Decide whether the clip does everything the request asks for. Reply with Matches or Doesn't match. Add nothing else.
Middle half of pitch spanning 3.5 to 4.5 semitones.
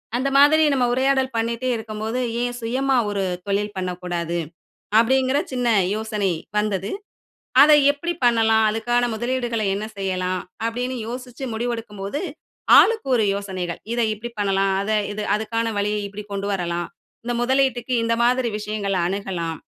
Matches